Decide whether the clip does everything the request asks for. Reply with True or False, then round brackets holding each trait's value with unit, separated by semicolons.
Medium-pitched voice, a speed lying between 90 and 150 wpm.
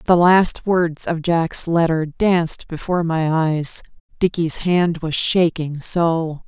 True (165 Hz; 140 wpm)